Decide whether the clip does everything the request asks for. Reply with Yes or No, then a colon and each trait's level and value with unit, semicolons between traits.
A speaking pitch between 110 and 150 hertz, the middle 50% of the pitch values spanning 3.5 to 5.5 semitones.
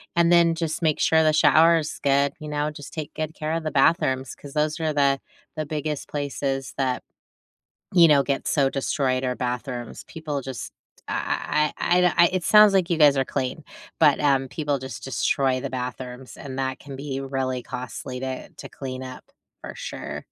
No: medium, 140 Hz; average, 2.8 semitones